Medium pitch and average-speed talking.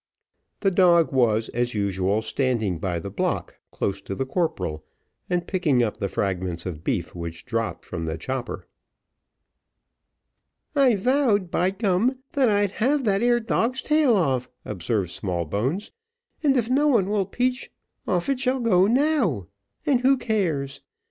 Yes: medium, 175 Hz; average, 150 wpm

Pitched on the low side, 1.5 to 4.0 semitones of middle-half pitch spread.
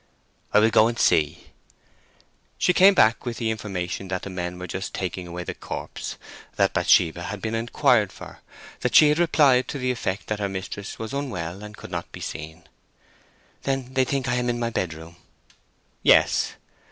No: low, 105 Hz; wide, 5.6 semitones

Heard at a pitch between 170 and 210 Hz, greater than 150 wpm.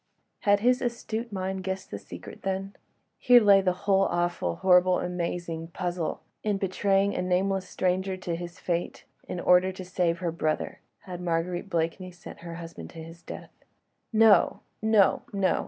Yes: medium, 185 Hz; average, 160 wpm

